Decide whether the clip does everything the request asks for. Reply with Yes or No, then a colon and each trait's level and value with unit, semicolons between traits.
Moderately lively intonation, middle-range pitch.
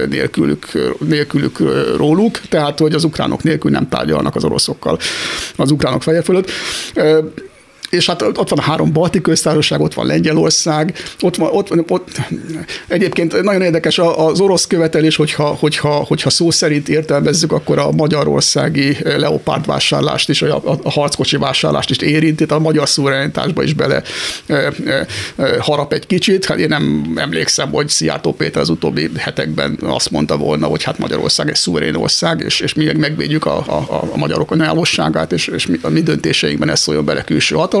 No: narrow, 2.2 semitones; medium, 155 Hz